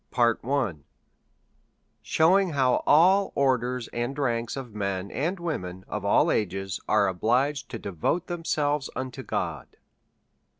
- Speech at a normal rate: No, slow, 120 wpm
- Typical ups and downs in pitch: No, wide, 6.3 semitones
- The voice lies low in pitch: Yes, low, 125 Hz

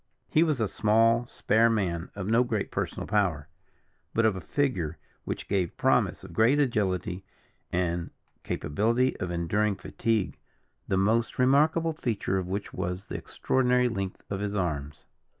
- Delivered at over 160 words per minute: No, average, 150 wpm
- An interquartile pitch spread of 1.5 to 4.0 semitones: No, average, 4.5 semitones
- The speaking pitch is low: Yes, low, 105 Hz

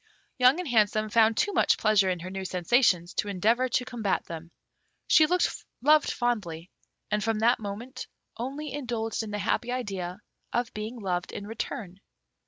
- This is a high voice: Yes, high, 220 Hz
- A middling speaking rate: Yes, average, 165 wpm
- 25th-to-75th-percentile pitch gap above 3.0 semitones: Yes, average, 4.3 semitones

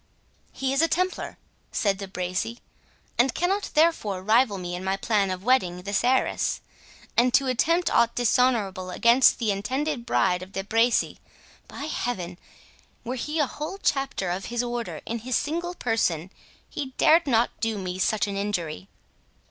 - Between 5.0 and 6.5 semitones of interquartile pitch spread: Yes, wide, 5.4 semitones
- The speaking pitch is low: No, high, 235 Hz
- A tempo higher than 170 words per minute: No, average, 155 wpm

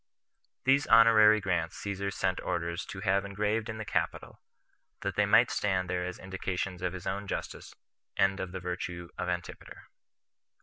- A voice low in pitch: Yes, very low, 95 Hz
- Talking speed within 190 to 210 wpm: No, average, 165 wpm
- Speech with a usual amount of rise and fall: No, narrow, 2.3 semitones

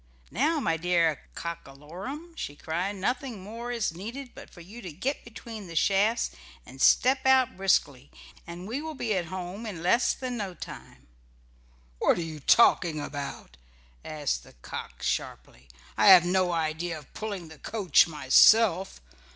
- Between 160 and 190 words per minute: Yes, average, 165 wpm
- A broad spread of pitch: Yes, wide, 6.1 semitones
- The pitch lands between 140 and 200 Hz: Yes, medium, 185 Hz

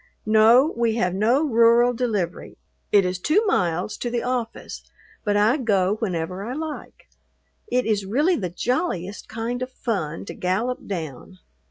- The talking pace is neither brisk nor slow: Yes, average, 155 wpm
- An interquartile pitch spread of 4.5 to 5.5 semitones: Yes, average, 4.8 semitones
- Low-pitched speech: No, high, 220 Hz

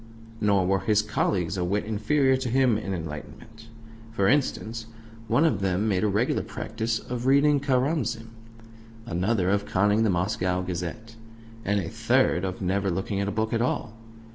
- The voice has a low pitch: Yes, low, 105 Hz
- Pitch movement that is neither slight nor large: Yes, average, 3.5 semitones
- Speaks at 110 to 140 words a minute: No, average, 165 wpm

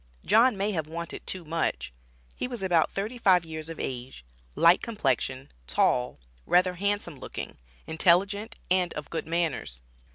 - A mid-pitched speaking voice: Yes, medium, 170 Hz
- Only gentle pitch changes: No, average, 4.0 semitones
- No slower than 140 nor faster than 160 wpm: Yes, average, 150 wpm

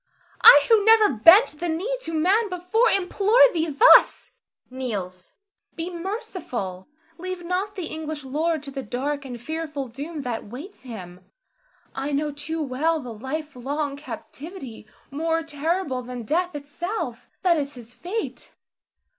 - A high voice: Yes, very high, 310 Hz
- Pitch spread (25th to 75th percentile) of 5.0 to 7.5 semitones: Yes, average, 5.3 semitones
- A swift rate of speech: No, average, 145 wpm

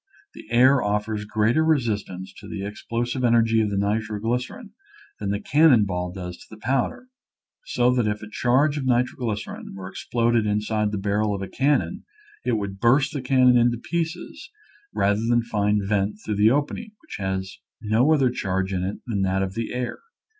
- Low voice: Yes, low, 110 Hz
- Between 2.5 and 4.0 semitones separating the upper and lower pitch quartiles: Yes, average, 3.6 semitones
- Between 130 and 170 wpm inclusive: No, average, 185 wpm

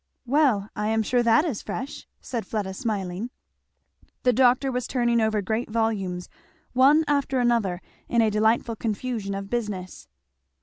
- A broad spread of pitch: No, average, 3.3 semitones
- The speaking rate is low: No, average, 145 wpm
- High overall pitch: Yes, high, 225 Hz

